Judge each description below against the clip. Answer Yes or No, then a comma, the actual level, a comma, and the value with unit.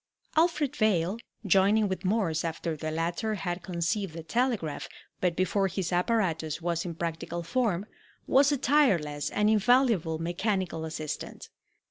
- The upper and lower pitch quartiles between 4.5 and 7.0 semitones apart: Yes, average, 4.8 semitones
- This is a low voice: No, medium, 185 Hz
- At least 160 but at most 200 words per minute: No, slow, 135 wpm